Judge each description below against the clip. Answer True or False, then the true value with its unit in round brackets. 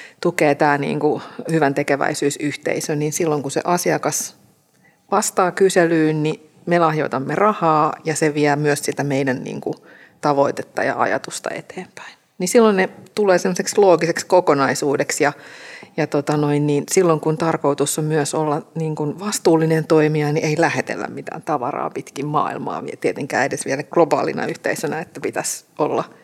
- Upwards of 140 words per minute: True (150 wpm)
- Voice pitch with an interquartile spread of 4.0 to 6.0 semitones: False (2.7 semitones)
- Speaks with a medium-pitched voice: True (155 Hz)